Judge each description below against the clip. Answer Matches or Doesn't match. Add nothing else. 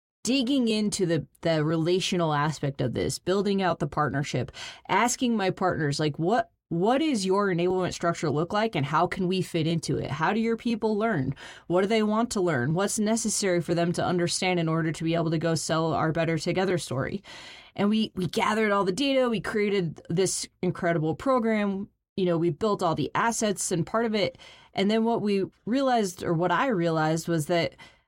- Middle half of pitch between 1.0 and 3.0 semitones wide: Doesn't match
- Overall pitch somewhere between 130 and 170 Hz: Doesn't match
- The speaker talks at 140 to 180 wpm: Doesn't match